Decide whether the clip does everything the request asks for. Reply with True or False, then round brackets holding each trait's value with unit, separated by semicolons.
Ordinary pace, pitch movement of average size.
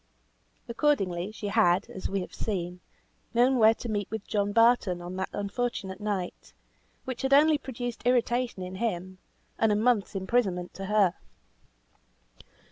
True (145 wpm; 4.3 semitones)